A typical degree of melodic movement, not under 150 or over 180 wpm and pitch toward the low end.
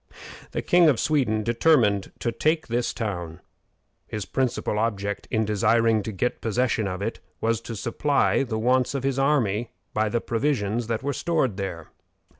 Yes: average, 3.6 semitones; average, 165 wpm; low, 115 Hz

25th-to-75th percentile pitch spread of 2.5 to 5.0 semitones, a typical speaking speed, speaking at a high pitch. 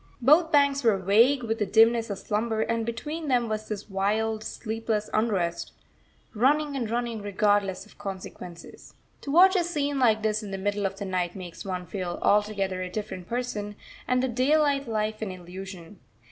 Yes: average, 3.9 semitones; average, 175 wpm; high, 215 Hz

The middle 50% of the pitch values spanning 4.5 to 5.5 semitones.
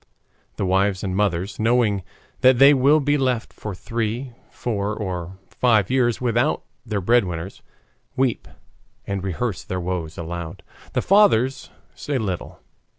Yes: average, 4.9 semitones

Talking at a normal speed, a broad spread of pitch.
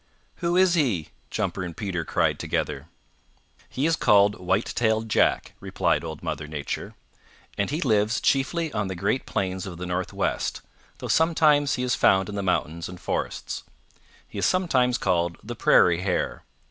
Yes: average, 165 wpm; wide, 6.9 semitones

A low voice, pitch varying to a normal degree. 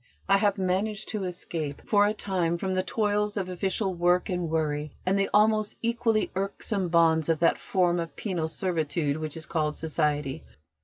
No: medium, 180 Hz; average, 3.8 semitones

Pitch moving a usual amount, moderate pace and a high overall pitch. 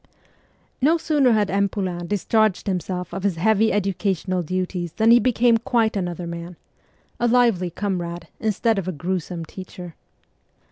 Yes: average, 3.9 semitones; average, 145 wpm; high, 195 Hz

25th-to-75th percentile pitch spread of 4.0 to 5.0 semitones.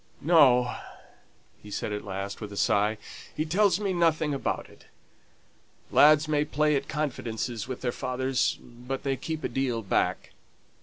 Yes: average, 4.5 semitones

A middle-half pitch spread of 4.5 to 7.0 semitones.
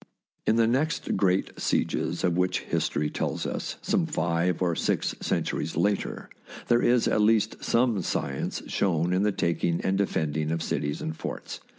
Yes: average, 5.2 semitones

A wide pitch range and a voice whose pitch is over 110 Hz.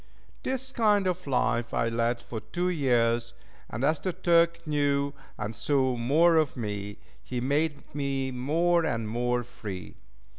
Yes: wide, 6.0 semitones; medium, 140 Hz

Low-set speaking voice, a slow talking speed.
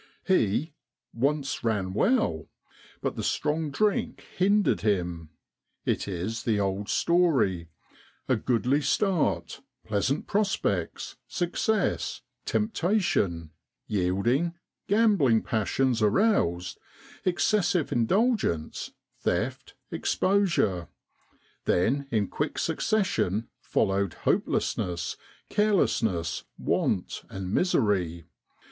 Yes: low, 115 Hz; slow, 85 wpm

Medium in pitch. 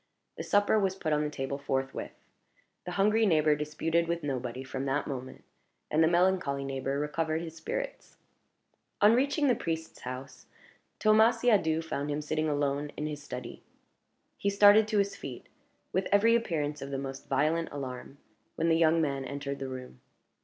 Yes: medium, 155 Hz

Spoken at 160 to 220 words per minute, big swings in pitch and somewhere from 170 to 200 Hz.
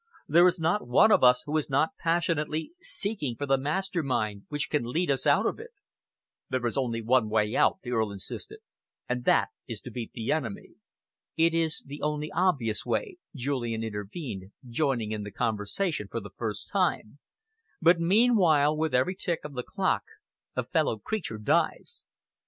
No: average, 175 wpm; wide, 6.3 semitones; medium, 140 Hz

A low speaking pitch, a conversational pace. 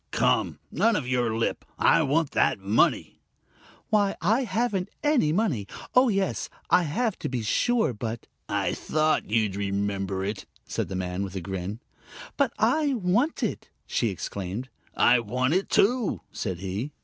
Yes: low, 125 Hz; average, 160 wpm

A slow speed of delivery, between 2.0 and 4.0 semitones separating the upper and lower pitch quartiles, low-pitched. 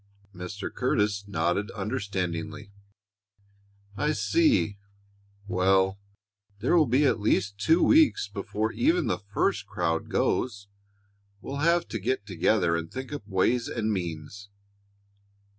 No: slow, 120 wpm; average, 5.2 semitones; low, 105 Hz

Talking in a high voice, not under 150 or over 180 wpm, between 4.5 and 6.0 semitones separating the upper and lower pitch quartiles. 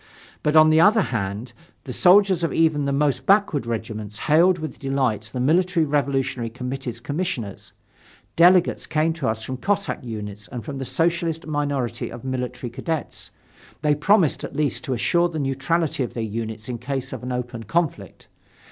No: medium, 140 Hz; average, 165 wpm; average, 5.2 semitones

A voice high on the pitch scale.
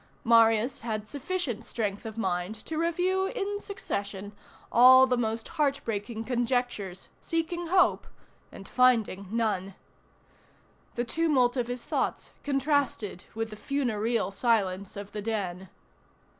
Yes: high, 230 Hz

